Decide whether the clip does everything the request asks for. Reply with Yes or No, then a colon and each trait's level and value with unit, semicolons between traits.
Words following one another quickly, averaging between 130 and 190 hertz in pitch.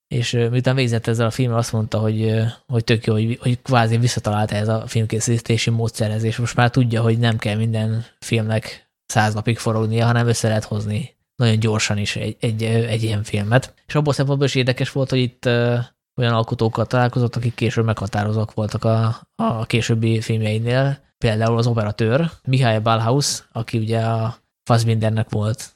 No: fast, 170 wpm; low, 115 Hz